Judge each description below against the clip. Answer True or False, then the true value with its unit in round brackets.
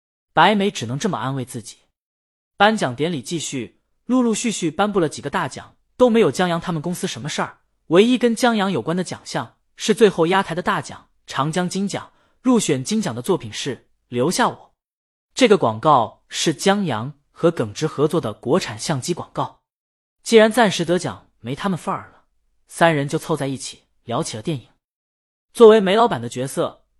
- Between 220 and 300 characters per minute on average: True (275 characters per minute)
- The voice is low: False (165 Hz)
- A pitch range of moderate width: False (7.3 semitones)